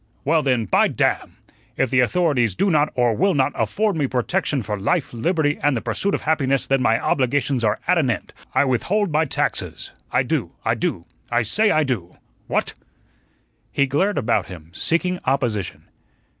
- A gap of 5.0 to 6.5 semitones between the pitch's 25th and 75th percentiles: Yes, wide, 5.4 semitones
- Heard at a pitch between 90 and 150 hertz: Yes, low, 135 Hz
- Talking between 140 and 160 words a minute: No, average, 180 wpm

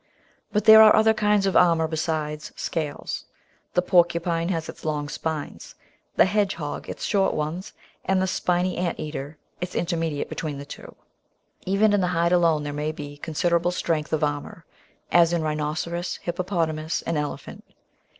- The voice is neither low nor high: Yes, medium, 170 Hz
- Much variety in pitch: No, average, 2.9 semitones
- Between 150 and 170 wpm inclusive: Yes, average, 160 wpm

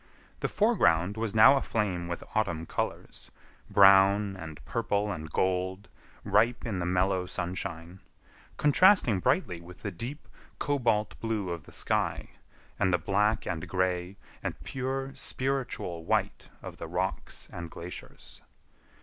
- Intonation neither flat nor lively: Yes, average, 4.3 semitones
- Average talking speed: No, slow, 130 wpm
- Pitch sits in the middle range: No, very low, 95 Hz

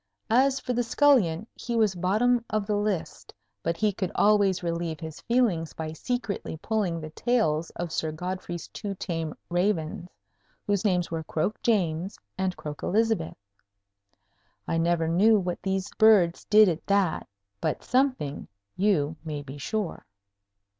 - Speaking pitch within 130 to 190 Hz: Yes, medium, 185 Hz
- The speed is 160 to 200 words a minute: No, average, 145 wpm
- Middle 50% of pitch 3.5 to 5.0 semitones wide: Yes, average, 4.7 semitones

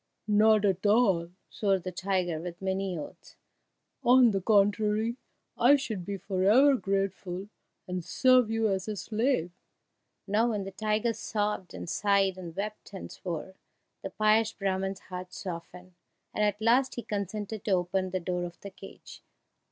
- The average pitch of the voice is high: Yes, high, 200 Hz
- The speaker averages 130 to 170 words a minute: Yes, average, 160 wpm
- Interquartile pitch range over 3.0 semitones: No, average, 2.7 semitones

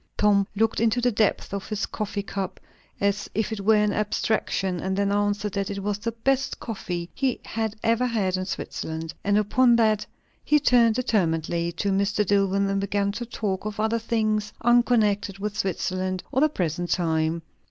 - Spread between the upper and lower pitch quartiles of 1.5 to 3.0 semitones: Yes, narrow, 2.5 semitones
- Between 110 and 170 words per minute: No, average, 180 wpm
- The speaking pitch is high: Yes, high, 205 Hz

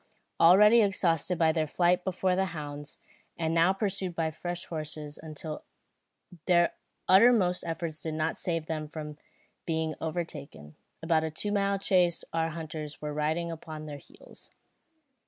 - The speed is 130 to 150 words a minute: Yes, average, 140 wpm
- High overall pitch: No, medium, 165 Hz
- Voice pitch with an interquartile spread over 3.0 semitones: No, average, 2.7 semitones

